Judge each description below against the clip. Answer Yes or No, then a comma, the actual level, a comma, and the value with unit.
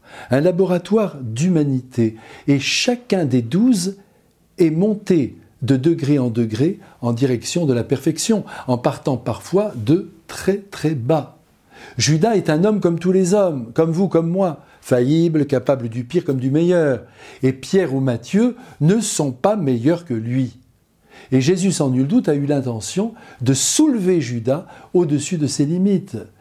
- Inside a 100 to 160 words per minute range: Yes, average, 155 wpm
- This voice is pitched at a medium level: Yes, medium, 155 Hz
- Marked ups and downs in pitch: Yes, wide, 6.3 semitones